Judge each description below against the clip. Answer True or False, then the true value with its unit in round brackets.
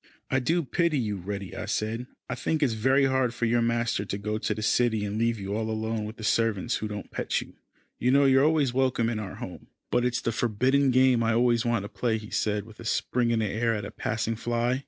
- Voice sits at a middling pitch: False (115 Hz)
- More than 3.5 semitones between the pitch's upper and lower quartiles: False (2.7 semitones)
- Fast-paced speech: True (260 wpm)